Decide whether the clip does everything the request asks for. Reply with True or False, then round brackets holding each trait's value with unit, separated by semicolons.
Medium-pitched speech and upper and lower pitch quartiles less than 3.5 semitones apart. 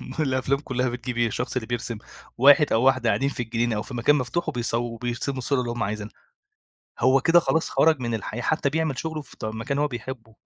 False (125 Hz; 3.0 semitones)